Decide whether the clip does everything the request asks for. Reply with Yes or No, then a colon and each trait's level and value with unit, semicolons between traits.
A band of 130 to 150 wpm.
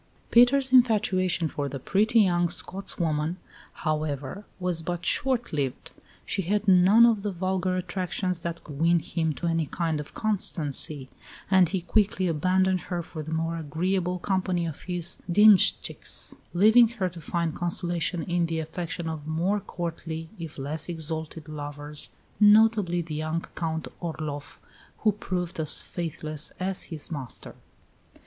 Yes: average, 145 wpm